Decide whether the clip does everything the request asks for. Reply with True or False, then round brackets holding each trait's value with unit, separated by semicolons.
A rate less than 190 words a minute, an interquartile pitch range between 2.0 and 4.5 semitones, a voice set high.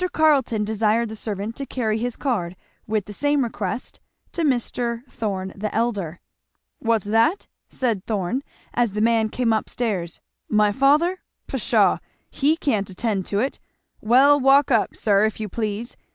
True (155 wpm; 3.6 semitones; 225 Hz)